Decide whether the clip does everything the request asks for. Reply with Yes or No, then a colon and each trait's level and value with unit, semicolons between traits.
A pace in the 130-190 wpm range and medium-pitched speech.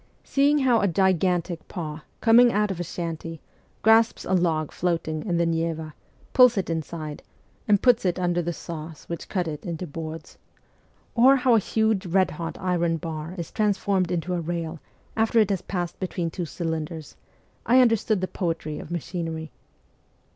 Yes: average, 170 wpm; medium, 175 Hz